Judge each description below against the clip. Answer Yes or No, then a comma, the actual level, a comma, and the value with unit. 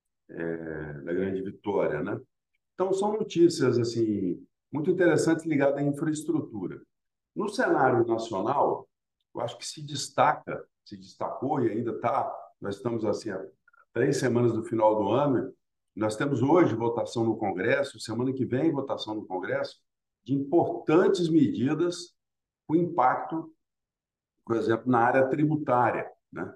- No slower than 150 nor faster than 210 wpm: No, average, 135 wpm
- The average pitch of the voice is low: Yes, low, 125 Hz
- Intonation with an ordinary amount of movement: No, wide, 6.0 semitones